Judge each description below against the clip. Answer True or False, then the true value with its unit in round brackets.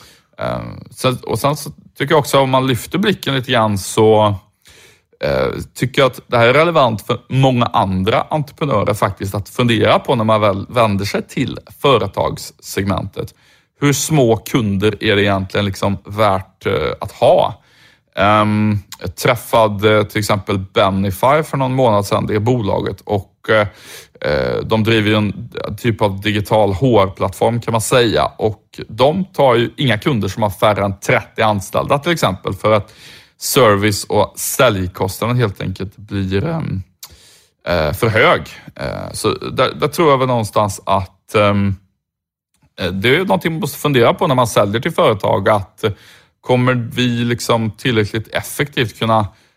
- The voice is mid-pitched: False (110 Hz)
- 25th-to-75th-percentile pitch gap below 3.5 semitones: False (3.8 semitones)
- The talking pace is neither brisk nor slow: True (150 wpm)